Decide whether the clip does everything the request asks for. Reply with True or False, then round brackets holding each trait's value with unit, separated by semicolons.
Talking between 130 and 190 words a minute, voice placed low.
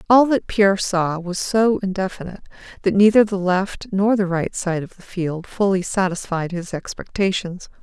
False (170 wpm; 190 Hz)